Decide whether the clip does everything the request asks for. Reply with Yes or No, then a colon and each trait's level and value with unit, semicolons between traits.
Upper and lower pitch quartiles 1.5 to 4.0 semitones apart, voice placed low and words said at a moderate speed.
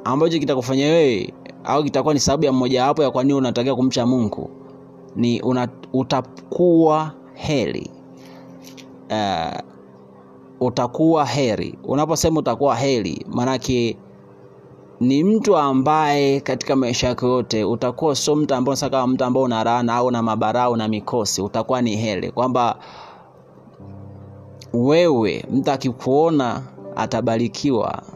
Yes: average, 3.2 semitones; low, 125 Hz; average, 115 wpm